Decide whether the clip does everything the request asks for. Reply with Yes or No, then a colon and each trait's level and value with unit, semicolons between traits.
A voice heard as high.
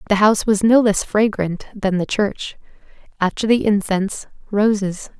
Yes: high, 205 Hz